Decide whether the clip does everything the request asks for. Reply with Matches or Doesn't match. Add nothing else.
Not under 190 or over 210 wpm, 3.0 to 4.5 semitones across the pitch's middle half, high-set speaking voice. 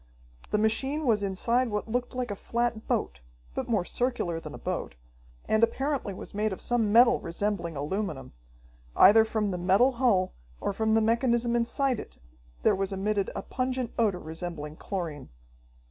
Doesn't match